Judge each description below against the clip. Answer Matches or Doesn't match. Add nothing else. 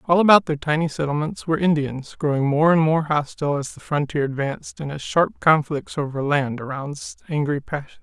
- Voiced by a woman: Doesn't match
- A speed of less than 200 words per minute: Matches